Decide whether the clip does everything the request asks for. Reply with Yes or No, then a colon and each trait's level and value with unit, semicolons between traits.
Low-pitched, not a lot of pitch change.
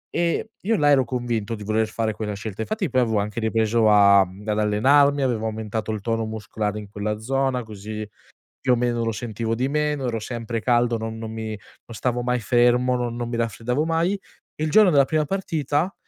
No: low, 115 Hz; average, 3.5 semitones